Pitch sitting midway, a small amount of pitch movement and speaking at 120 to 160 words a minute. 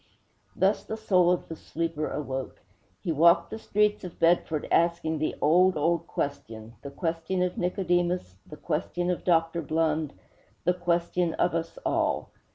Yes: medium, 170 Hz; narrow, 2.3 semitones; average, 155 wpm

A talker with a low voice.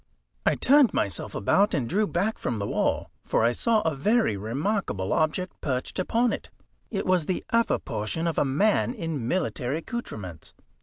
No: medium, 165 Hz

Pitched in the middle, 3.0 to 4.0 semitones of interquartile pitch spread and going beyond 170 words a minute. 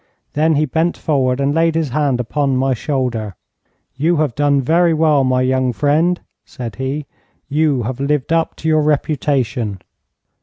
No: medium, 145 Hz; average, 3.3 semitones; average, 160 wpm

